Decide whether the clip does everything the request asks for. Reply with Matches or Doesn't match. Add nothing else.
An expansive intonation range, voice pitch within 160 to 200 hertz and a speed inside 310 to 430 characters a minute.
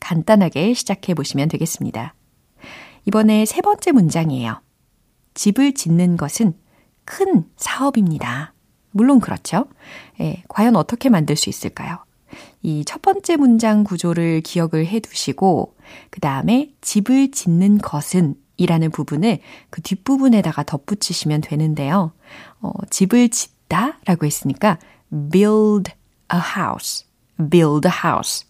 Doesn't match